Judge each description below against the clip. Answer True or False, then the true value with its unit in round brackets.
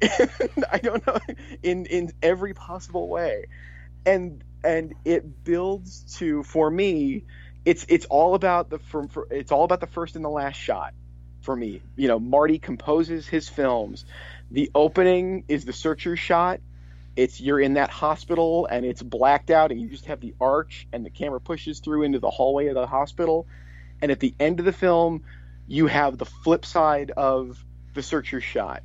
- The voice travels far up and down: True (6.2 semitones)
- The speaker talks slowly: False (180 wpm)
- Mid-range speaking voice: True (150 Hz)